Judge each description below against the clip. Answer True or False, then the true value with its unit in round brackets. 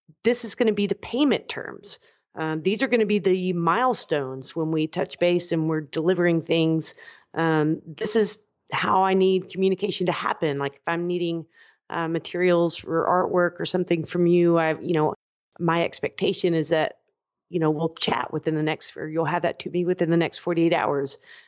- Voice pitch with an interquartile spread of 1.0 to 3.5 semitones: True (2.4 semitones)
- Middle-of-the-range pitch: True (170 Hz)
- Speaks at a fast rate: False (195 wpm)